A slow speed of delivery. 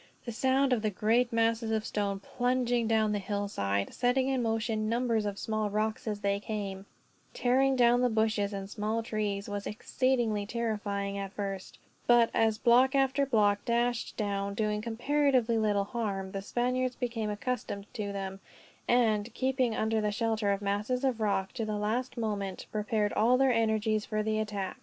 No: average, 170 wpm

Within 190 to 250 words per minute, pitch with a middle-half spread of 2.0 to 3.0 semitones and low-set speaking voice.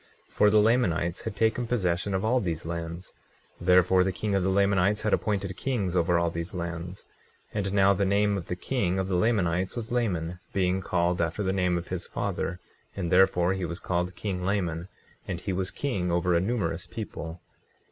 Yes: average, 200 wpm; narrow, 2.5 semitones; very low, 95 Hz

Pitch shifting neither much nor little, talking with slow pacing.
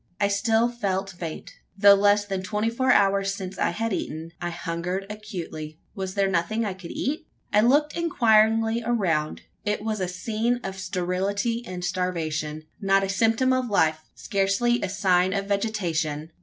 No: average, 3.5 semitones; average, 165 wpm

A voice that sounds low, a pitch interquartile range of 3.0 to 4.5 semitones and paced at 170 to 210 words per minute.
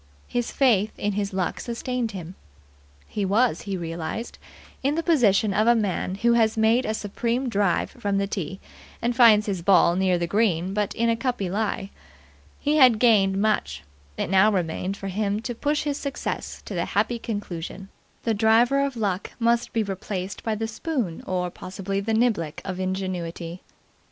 No: high, 205 Hz; average, 3.7 semitones; average, 175 wpm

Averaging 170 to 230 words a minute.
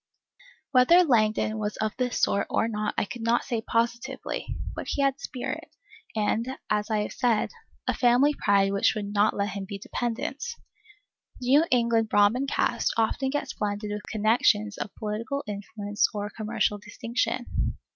No: average, 160 wpm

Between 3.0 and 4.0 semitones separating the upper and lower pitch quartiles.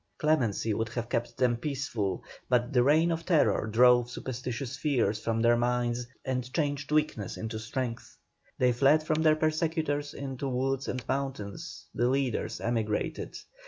Yes: average, 3.5 semitones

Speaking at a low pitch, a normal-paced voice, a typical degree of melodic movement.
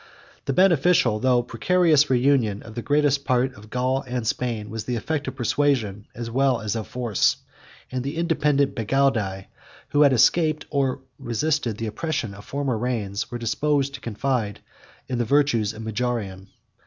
Yes: low, 125 Hz; average, 165 wpm; average, 4.1 semitones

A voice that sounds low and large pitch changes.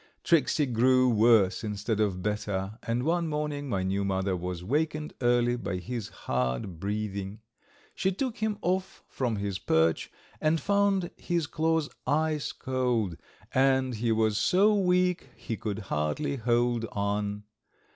Yes: low, 120 Hz; wide, 7.2 semitones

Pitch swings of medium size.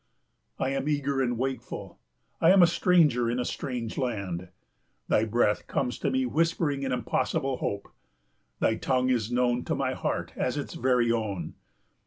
Yes: average, 3.2 semitones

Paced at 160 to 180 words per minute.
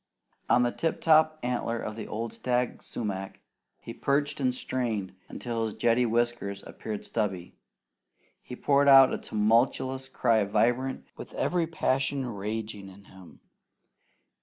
No: slow, 135 wpm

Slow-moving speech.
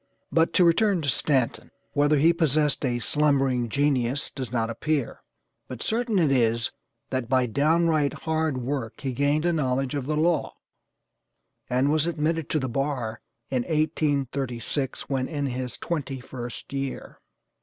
No: average, 155 wpm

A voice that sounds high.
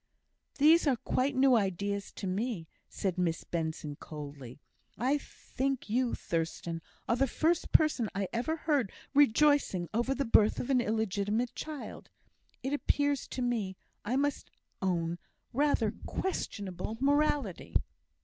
Yes: high, 235 Hz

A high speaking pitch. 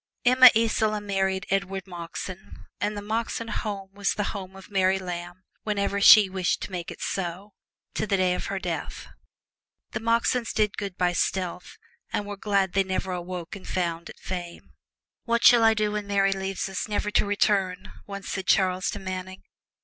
Yes: high, 195 Hz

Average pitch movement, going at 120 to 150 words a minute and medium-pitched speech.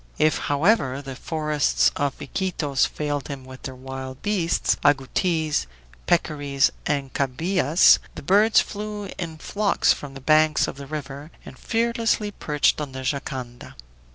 Yes: average, 4.3 semitones; average, 140 wpm; medium, 150 Hz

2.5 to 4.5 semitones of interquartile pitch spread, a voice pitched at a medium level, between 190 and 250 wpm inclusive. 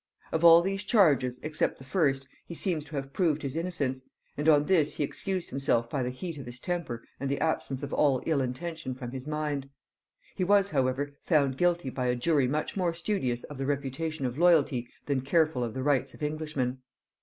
Yes: average, 4.0 semitones; medium, 145 Hz; fast, 205 wpm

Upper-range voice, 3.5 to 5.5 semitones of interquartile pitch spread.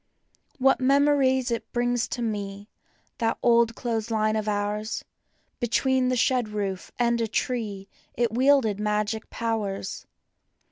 No: high, 230 Hz; average, 2.8 semitones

